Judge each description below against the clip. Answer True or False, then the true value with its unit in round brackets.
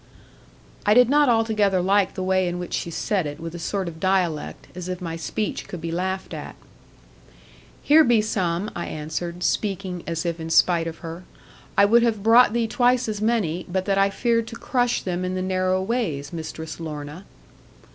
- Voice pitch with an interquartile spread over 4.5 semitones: False (4.2 semitones)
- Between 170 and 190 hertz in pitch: True (185 Hz)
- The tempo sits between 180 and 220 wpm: True (195 wpm)